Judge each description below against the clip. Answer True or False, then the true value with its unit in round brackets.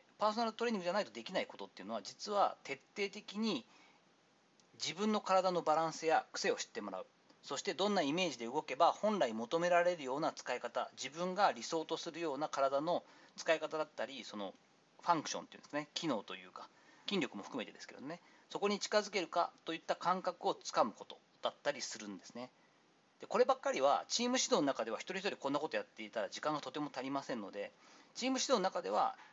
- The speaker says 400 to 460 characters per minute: True (445 characters per minute)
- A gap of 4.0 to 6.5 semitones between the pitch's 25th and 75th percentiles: True (5.5 semitones)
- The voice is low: False (180 Hz)